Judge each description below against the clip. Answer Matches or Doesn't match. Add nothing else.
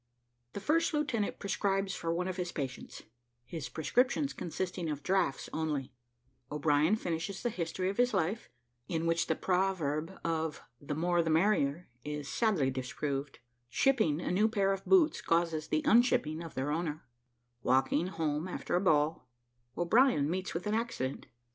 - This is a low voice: Doesn't match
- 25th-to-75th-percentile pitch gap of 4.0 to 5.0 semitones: Matches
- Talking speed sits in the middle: Matches